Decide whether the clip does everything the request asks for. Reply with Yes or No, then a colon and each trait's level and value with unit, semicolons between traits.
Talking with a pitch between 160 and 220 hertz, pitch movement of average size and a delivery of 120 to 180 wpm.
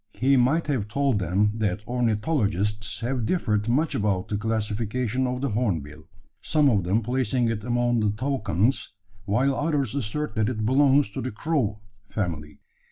No: low, 115 Hz; average, 4.0 semitones; average, 160 wpm